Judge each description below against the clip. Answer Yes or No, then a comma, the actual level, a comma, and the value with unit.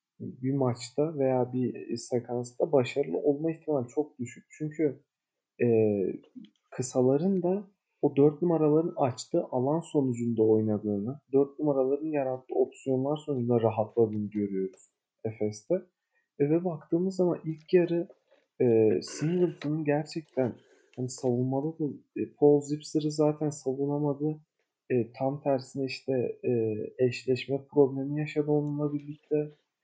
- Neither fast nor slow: Yes, average, 110 wpm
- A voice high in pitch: No, medium, 140 Hz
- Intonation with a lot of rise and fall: No, average, 3.5 semitones